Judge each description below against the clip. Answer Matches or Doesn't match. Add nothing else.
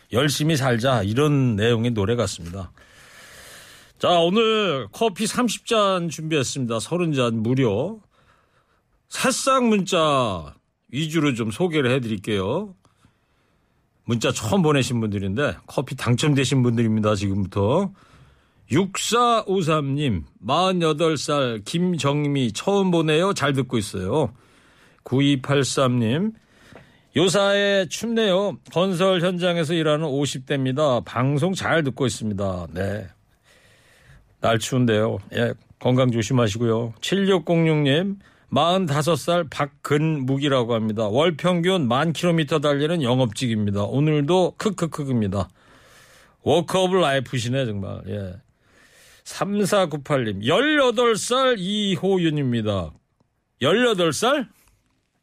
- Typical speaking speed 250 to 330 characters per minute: Doesn't match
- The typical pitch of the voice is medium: Matches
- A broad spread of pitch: Matches